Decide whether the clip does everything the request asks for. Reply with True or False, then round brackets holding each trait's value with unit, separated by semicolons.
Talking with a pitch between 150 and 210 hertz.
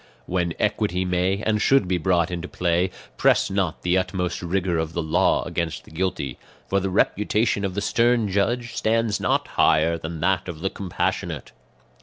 False (95 Hz)